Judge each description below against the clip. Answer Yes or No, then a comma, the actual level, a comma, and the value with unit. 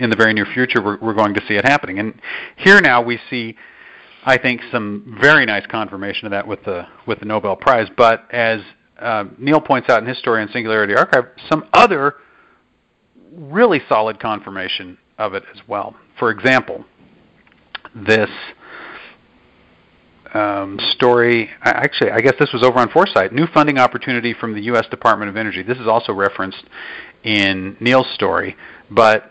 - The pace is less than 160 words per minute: No, average, 165 wpm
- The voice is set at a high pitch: No, low, 115 Hz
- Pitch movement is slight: No, average, 3.4 semitones